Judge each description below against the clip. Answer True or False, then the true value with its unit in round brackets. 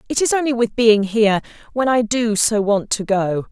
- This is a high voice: True (220 Hz)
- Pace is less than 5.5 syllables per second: True (5.0 syllables/s)